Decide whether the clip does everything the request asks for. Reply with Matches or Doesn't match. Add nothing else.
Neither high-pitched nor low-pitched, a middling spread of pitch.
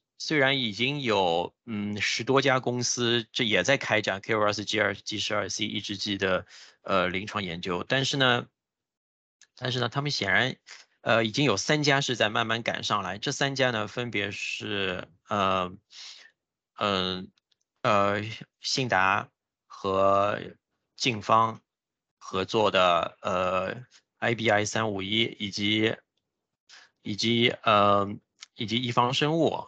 Doesn't match